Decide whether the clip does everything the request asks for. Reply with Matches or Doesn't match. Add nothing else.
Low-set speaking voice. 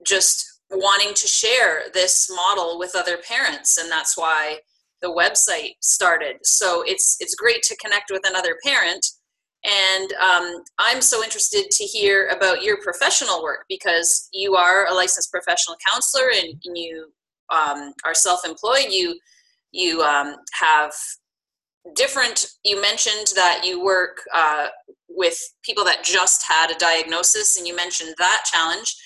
Doesn't match